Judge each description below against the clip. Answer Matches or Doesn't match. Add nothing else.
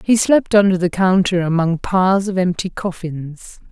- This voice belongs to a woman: Matches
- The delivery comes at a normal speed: Matches